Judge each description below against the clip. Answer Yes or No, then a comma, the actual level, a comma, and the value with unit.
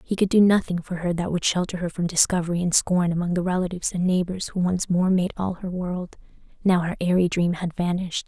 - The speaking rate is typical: No, fast, 230 wpm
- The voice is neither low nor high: Yes, medium, 180 Hz